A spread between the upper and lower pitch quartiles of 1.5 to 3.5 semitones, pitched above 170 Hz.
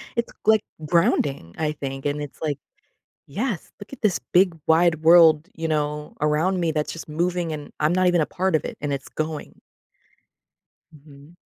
No: average, 2.9 semitones; medium, 160 Hz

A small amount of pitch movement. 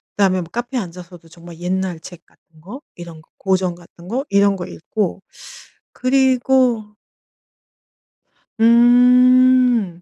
No: wide, 6.0 semitones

